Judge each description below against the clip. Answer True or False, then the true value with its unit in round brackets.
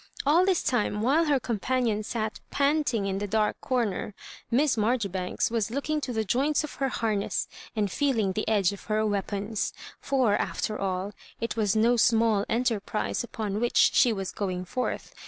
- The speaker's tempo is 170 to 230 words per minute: True (175 wpm)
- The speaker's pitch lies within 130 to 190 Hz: False (220 Hz)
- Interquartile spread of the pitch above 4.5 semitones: False (3.8 semitones)